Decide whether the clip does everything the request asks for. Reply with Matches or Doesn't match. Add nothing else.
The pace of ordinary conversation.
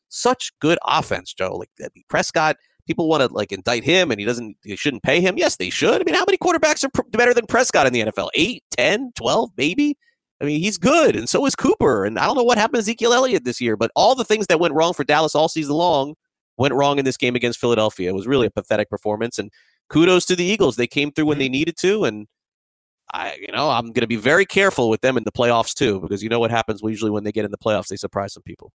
Doesn't match